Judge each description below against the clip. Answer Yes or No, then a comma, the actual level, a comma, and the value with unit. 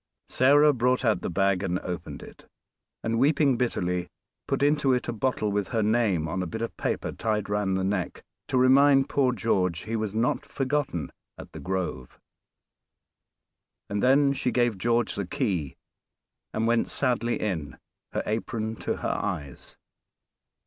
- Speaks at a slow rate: No, average, 160 wpm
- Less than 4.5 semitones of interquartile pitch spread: No, average, 5.1 semitones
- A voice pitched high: No, low, 110 Hz